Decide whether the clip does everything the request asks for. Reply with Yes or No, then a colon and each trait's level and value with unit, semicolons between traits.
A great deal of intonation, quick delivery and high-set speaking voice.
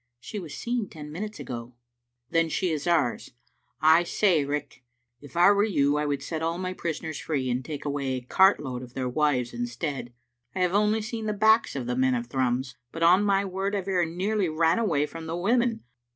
No: wide, 6.5 semitones; fast, 220 wpm; medium, 160 Hz